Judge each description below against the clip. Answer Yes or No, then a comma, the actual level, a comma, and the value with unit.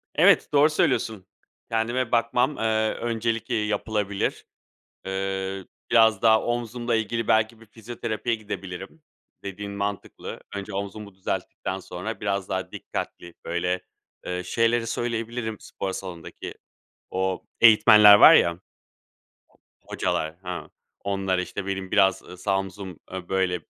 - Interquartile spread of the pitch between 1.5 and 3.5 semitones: Yes, average, 3.0 semitones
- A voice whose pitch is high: No, low, 100 Hz